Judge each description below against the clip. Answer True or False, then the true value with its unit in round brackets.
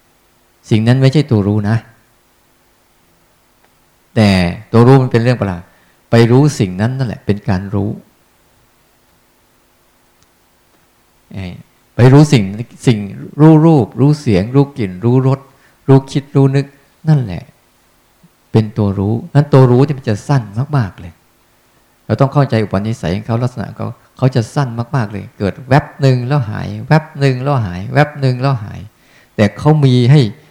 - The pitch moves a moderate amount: True (5.0 semitones)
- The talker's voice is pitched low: True (120 Hz)